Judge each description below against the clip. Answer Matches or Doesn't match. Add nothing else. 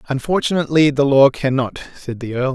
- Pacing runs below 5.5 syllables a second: Doesn't match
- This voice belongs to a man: Matches